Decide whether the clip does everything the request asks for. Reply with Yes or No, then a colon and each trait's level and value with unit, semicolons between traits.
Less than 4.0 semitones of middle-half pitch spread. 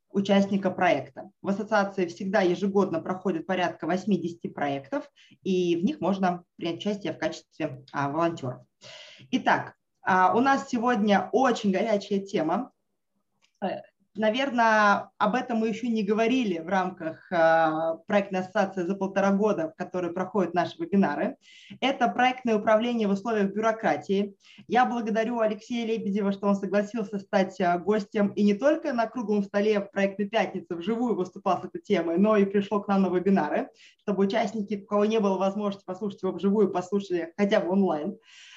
Yes: average, 2.8 semitones